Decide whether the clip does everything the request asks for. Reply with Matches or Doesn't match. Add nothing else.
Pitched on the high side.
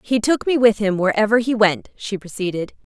Matches